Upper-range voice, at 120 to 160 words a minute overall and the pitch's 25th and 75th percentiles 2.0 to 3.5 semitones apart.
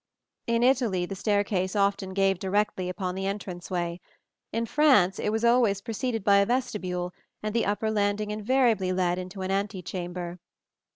Yes: high, 200 Hz; average, 155 wpm; average, 2.9 semitones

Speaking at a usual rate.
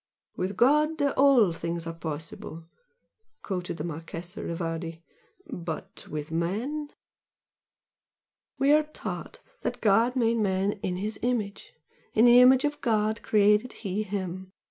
No: slow, 130 wpm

